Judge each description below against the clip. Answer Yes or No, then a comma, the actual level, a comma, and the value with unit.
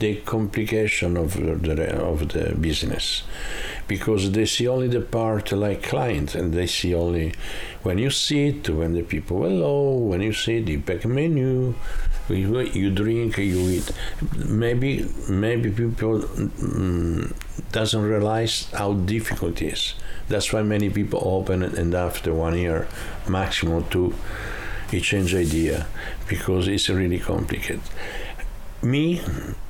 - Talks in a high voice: No, low, 100 Hz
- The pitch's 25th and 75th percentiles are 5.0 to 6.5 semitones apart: No, average, 4.1 semitones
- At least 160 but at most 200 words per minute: No, slow, 135 wpm